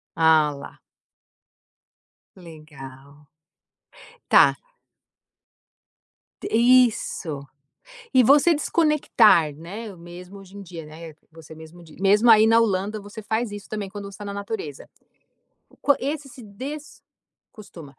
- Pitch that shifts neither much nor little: No, wide, 6.0 semitones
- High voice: Yes, high, 200 Hz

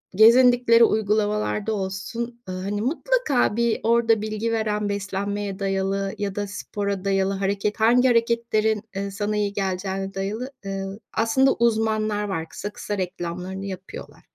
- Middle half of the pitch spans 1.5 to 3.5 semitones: Yes, narrow, 2.6 semitones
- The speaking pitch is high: Yes, high, 205 Hz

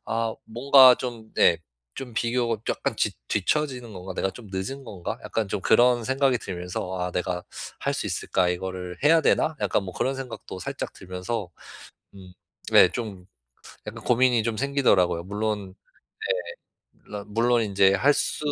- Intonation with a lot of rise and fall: No, average, 5.0 semitones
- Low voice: Yes, low, 110 Hz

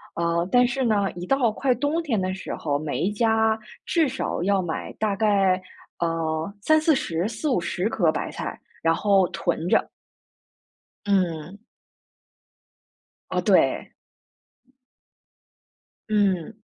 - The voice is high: Yes, high, 200 Hz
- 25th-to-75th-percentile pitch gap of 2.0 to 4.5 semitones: No, average, 5.1 semitones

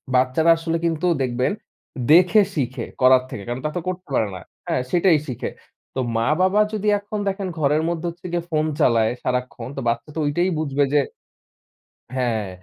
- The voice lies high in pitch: No, medium, 150 Hz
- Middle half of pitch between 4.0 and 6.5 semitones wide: Yes, wide, 5.5 semitones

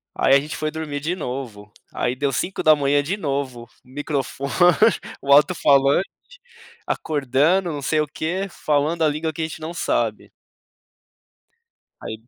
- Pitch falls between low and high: Yes, medium, 145 Hz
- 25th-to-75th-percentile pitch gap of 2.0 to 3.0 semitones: Yes, narrow, 2.6 semitones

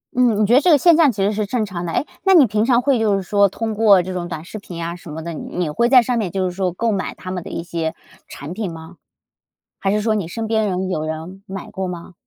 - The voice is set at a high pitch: Yes, high, 195 Hz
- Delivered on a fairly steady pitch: No, average, 4.2 semitones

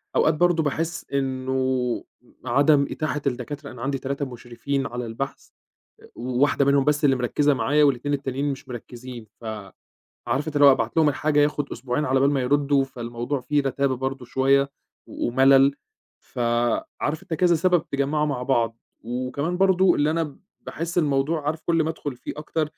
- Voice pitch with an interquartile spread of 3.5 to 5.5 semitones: No, average, 2.7 semitones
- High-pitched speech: No, medium, 140 Hz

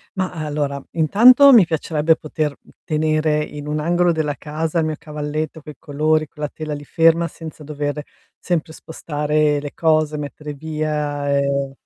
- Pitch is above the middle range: No, medium, 155 Hz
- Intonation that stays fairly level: Yes, narrow, 1.3 semitones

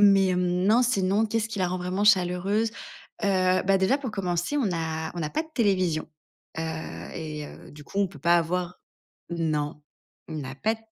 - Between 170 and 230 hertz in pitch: Yes, medium, 185 Hz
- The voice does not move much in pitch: No, average, 3.7 semitones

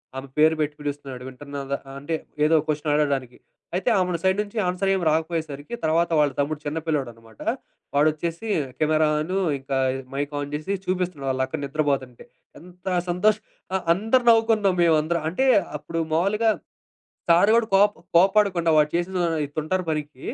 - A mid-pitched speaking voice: Yes, medium, 160 Hz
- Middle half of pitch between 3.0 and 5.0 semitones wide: Yes, average, 4.2 semitones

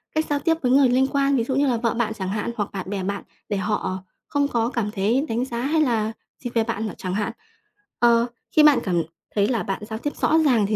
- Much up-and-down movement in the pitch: No, average, 4.3 semitones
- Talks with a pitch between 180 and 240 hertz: Yes, high, 230 Hz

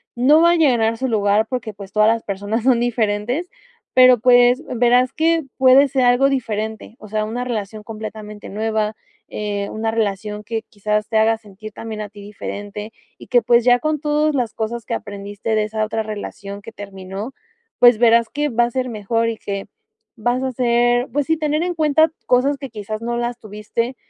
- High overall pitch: Yes, high, 225 Hz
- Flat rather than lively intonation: No, average, 3.0 semitones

